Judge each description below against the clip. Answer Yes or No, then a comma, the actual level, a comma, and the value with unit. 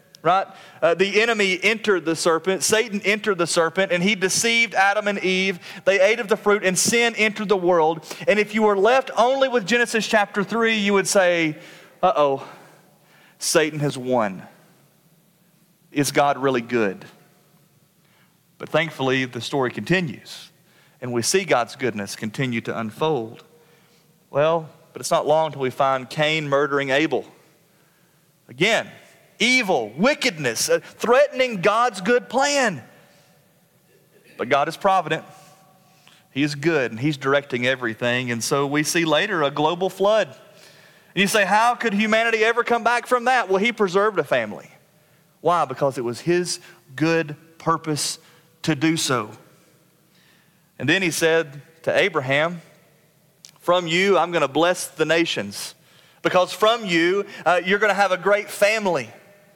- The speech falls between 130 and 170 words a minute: Yes, average, 150 wpm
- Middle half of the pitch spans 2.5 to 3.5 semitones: No, average, 4.6 semitones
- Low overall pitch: No, medium, 175 Hz